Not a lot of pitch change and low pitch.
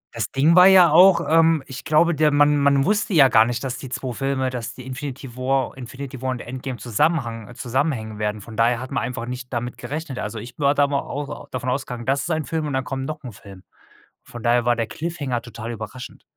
No: average, 3.3 semitones; low, 130 Hz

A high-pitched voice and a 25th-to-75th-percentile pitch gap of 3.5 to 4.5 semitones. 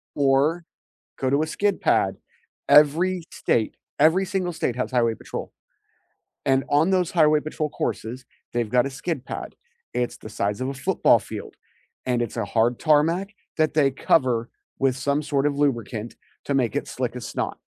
No: medium, 140 Hz; average, 4.2 semitones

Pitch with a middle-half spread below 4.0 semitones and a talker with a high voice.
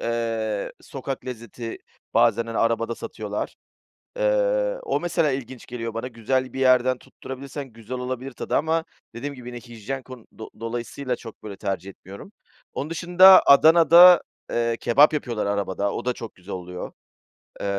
No: average, 3.5 semitones; low, 125 Hz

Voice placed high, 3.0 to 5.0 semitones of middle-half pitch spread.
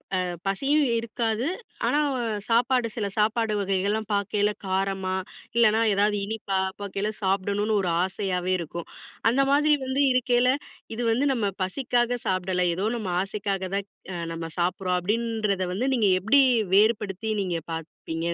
Yes: high, 205 Hz; average, 3.5 semitones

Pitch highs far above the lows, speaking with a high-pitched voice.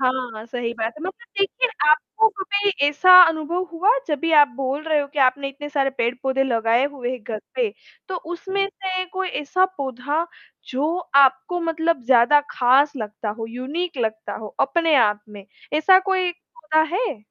Yes: wide, 5.8 semitones; very high, 290 Hz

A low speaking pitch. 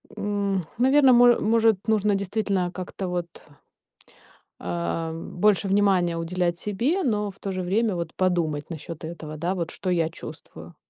No: medium, 185 Hz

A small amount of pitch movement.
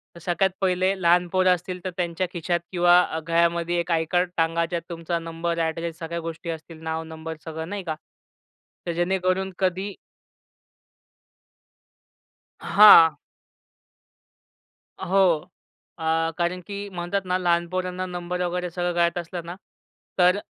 Yes: narrow, 1.6 semitones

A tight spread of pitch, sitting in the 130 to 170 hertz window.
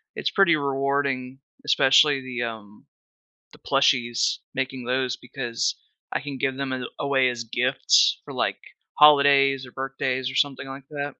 Yes: narrow, 1.7 semitones; low, 135 Hz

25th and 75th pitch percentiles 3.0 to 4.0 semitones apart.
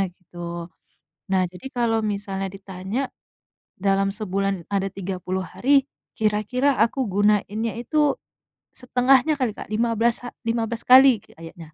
Yes: average, 3.7 semitones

